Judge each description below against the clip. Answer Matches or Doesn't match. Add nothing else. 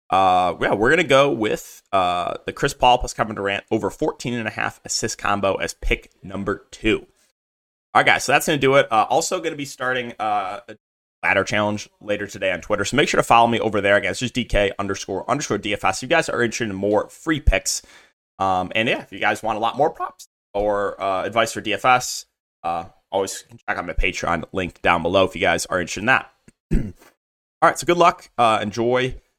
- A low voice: Matches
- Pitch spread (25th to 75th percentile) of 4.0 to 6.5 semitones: Matches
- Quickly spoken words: Matches